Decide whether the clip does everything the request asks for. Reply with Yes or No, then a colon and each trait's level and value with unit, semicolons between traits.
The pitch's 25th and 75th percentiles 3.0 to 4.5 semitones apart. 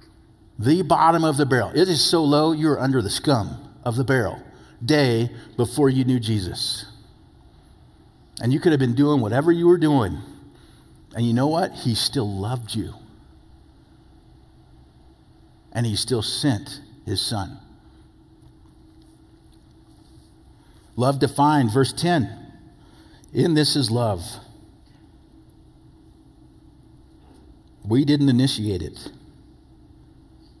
No: average, 5.1 semitones